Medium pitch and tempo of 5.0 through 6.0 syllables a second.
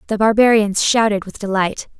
No: high, 210 Hz; 5.2 syllables/s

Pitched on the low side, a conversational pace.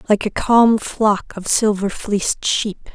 No: high, 210 Hz; average, 165 wpm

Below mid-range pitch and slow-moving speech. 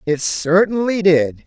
No: medium, 175 Hz; slow, 125 wpm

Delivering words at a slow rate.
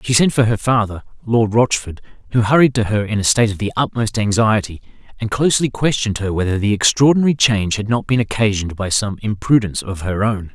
No: fast, 205 wpm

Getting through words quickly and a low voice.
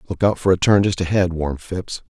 Yes: fast, 250 wpm; very low, 90 Hz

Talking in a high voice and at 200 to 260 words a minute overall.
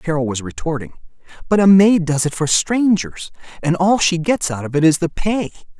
No: medium, 170 Hz; fast, 205 wpm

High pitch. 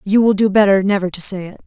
Yes: high, 195 Hz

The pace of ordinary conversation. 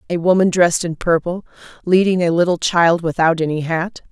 Yes: average, 175 wpm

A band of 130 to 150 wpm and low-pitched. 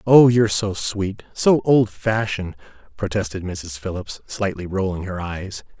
Yes: slow, 135 wpm; low, 100 Hz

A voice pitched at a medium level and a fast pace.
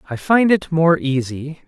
No: medium, 155 Hz; average, 180 wpm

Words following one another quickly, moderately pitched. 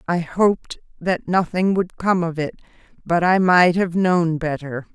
No: average, 170 wpm; medium, 175 Hz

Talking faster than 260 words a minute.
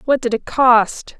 No: average, 200 wpm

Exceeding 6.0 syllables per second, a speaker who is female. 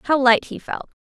No: 4.5 syllables/s; female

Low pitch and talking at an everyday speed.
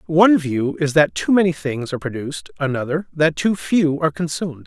No: medium, 150 Hz; average, 195 wpm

